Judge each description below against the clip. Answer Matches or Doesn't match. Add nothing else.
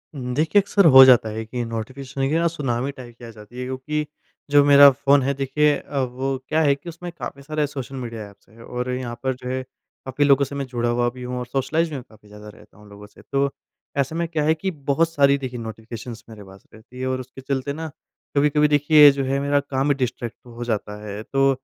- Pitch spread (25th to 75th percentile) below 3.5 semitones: Matches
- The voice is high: Doesn't match